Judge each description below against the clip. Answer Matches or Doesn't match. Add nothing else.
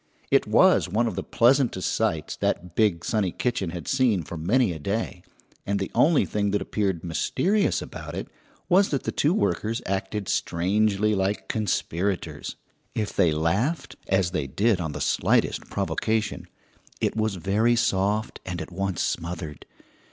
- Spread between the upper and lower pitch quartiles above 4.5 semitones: Doesn't match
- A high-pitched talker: Doesn't match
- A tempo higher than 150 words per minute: Matches